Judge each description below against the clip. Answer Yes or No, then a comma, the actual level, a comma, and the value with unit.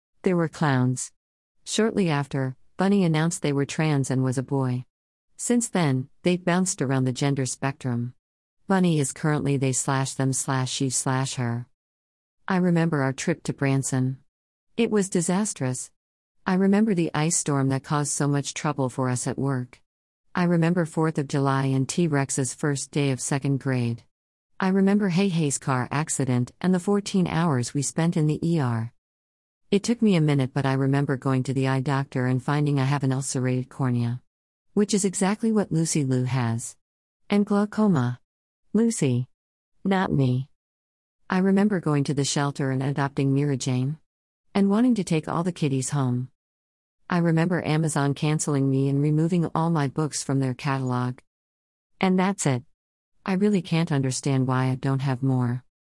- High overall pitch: No, medium, 140 Hz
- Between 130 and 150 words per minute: No, average, 170 wpm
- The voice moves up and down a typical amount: Yes, average, 4.5 semitones